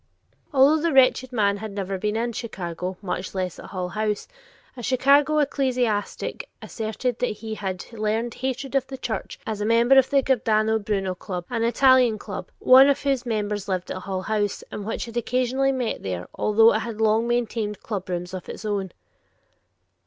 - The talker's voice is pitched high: Yes, high, 220 Hz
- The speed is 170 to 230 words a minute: Yes, average, 180 wpm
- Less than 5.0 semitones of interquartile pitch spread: Yes, average, 4.0 semitones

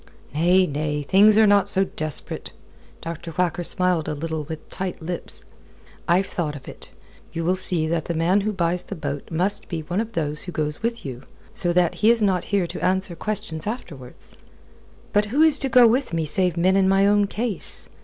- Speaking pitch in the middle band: Yes, medium, 180 Hz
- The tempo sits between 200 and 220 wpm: Yes, fast, 205 wpm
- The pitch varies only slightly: No, average, 4.1 semitones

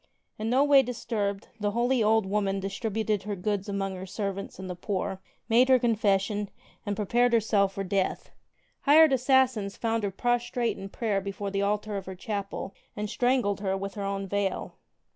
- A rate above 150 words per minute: Yes, average, 180 wpm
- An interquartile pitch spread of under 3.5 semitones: Yes, average, 2.9 semitones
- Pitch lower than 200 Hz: No, high, 205 Hz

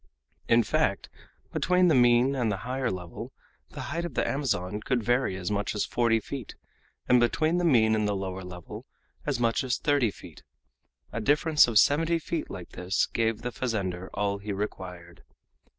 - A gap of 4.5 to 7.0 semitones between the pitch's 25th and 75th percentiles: Yes, average, 5.2 semitones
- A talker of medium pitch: No, low, 115 Hz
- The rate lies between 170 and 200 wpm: Yes, average, 180 wpm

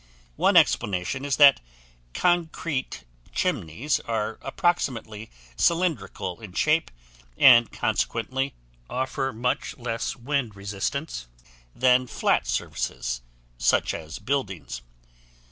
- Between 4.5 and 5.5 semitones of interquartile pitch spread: Yes, average, 5.1 semitones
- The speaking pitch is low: Yes, low, 125 Hz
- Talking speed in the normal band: No, slow, 95 wpm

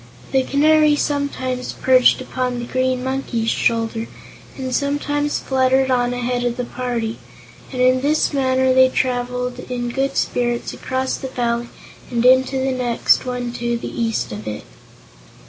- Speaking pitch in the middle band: No, very high, 255 Hz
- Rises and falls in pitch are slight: Yes, narrow, 1.5 semitones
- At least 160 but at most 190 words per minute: No, average, 150 wpm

